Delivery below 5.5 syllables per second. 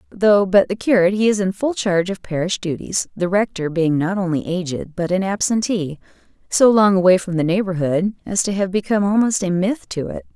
No: 5.6 syllables/s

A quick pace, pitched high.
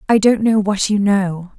Yes: fast, 225 wpm; high, 205 Hz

